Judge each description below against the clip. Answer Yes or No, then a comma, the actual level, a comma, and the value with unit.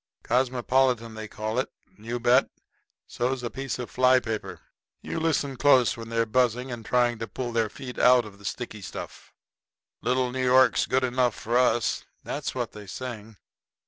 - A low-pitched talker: Yes, low, 120 Hz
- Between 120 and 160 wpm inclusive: No, average, 175 wpm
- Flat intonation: Yes, narrow, 2.1 semitones